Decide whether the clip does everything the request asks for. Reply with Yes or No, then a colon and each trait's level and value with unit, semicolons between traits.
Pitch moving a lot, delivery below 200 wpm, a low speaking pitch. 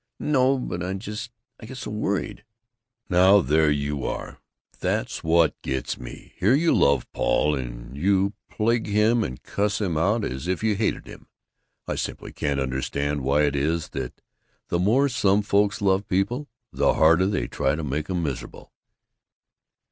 Yes: wide, 6.3 semitones; average, 170 wpm; very low, 95 Hz